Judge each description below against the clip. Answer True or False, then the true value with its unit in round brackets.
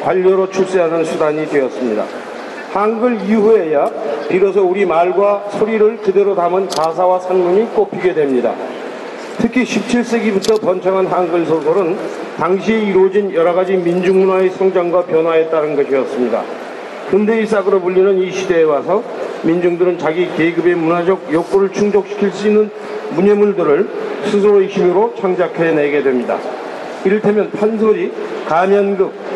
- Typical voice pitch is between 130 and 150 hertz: False (195 Hz)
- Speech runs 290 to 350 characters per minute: True (325 characters per minute)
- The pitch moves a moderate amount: True (3.3 semitones)